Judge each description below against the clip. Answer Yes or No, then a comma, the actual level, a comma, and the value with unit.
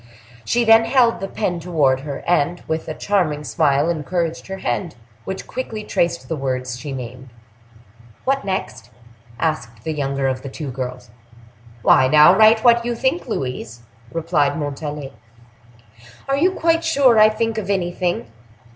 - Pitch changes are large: Yes, wide, 7.9 semitones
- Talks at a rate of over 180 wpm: No, average, 155 wpm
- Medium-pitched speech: Yes, medium, 165 Hz